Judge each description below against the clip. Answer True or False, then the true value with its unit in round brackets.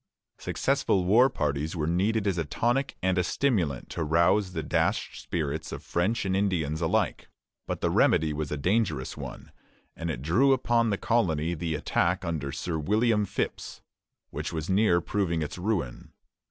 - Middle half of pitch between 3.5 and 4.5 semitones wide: False (5.0 semitones)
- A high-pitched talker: False (85 Hz)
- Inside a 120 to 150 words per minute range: False (165 wpm)